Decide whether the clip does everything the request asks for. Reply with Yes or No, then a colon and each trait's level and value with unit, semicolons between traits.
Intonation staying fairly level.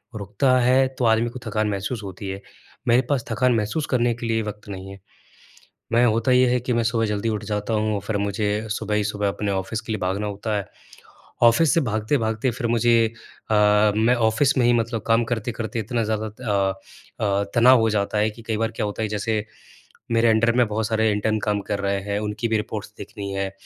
Yes: narrow, 2.2 semitones